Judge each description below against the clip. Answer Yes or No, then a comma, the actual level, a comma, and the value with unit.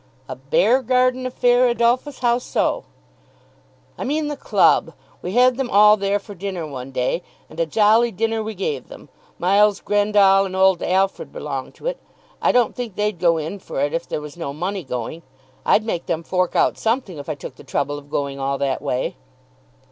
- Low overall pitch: No, high, 195 Hz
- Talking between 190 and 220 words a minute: Yes, average, 195 wpm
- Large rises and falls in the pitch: Yes, wide, 7.0 semitones